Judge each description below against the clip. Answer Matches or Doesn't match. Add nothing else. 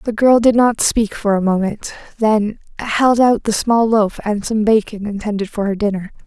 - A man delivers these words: Doesn't match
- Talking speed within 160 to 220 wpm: Matches